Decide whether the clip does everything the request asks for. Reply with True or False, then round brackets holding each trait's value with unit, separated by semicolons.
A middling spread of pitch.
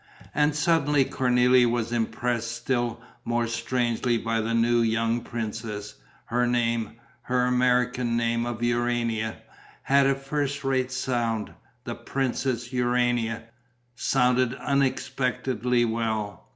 False (1.6 semitones)